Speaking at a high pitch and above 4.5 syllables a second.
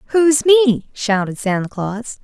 No: high, 235 Hz; 4.1 syllables/s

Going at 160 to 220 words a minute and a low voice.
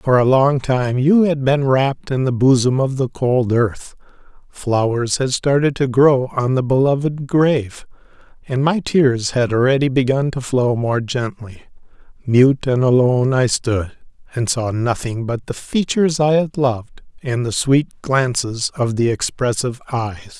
Yes: average, 165 wpm; low, 130 Hz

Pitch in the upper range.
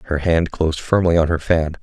No: very low, 80 Hz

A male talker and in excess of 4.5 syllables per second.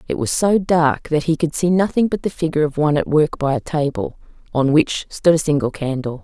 No: female; 5.6 syllables/s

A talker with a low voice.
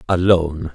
Yes: very low, 85 Hz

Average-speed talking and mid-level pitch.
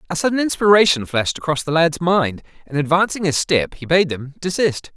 Yes: average, 195 wpm; medium, 160 Hz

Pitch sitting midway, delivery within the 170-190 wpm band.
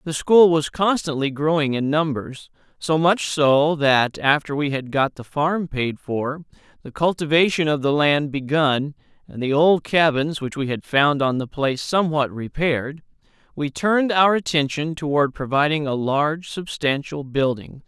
No: medium, 150 Hz; average, 160 wpm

